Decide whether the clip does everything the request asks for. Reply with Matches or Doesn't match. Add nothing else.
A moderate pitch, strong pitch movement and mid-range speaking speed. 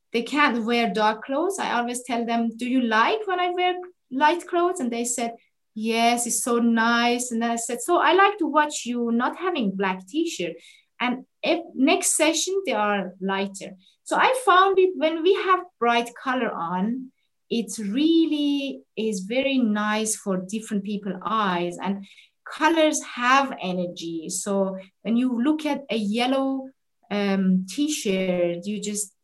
Doesn't match